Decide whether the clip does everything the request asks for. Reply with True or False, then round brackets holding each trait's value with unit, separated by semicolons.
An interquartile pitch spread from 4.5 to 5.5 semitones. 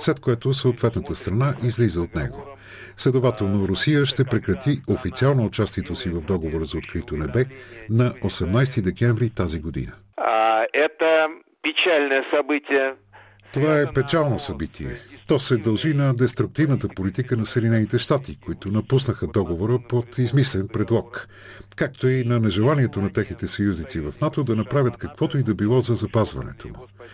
True (4.8 semitones)